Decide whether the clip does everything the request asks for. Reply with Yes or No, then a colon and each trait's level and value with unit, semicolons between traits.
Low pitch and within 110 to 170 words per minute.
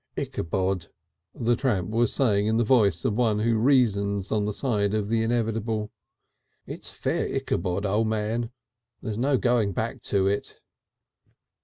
Yes: low, 110 Hz; average, 150 wpm